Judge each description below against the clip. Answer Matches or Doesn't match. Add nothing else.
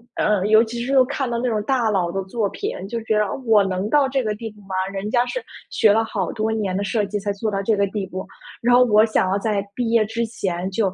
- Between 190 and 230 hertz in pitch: Matches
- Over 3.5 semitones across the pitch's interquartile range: Doesn't match